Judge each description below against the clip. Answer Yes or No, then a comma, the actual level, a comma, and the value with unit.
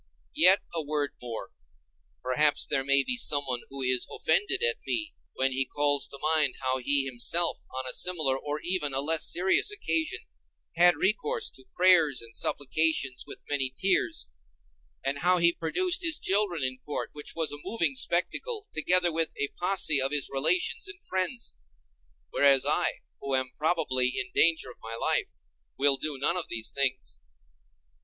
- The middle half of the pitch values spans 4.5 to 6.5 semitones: Yes, average, 5.2 semitones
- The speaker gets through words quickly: No, average, 165 wpm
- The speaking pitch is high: No, medium, 150 Hz